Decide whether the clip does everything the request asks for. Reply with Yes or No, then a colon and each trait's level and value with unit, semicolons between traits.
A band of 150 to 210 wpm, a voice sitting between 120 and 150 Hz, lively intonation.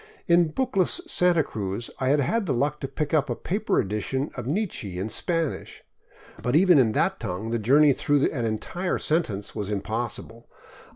Yes: average, 175 wpm; low, 135 Hz; wide, 7.0 semitones